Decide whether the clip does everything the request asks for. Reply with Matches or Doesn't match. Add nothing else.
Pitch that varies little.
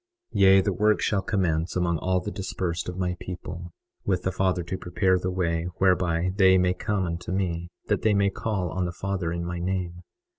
Matches